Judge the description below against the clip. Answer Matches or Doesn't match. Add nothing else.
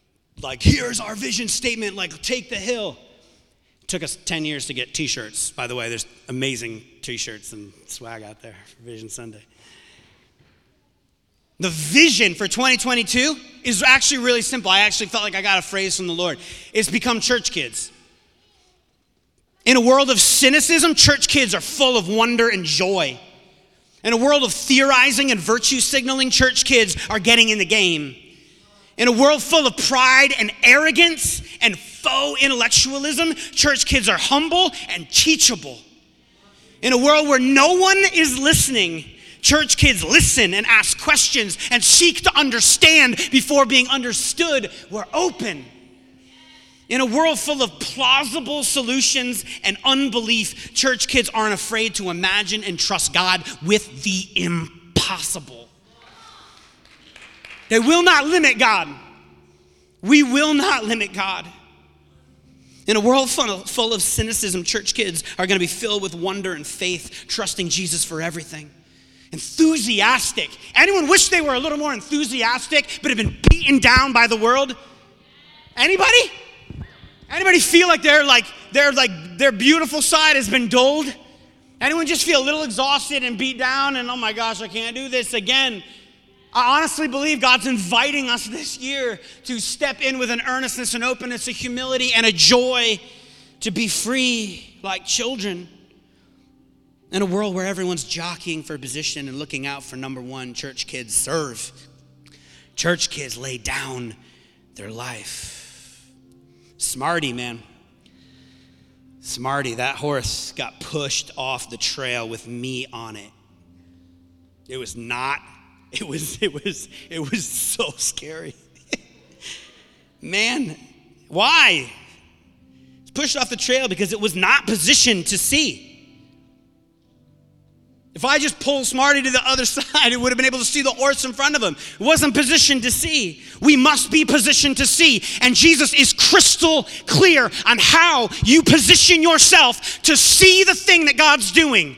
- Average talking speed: Matches